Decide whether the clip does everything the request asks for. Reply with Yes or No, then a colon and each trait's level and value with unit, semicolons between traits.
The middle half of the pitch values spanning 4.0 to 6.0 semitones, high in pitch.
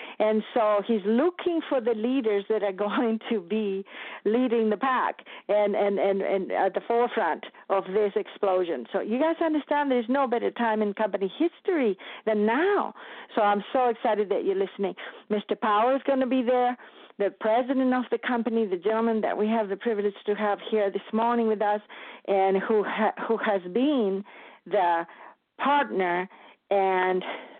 No: average, 3.3 semitones; high, 215 Hz